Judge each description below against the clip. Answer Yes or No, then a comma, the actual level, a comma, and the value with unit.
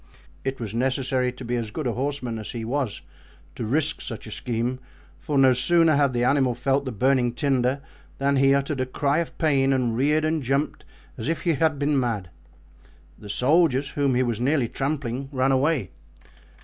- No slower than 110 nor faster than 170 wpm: No, average, 190 wpm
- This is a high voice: No, low, 135 Hz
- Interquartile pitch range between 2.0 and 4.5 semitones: Yes, narrow, 2.6 semitones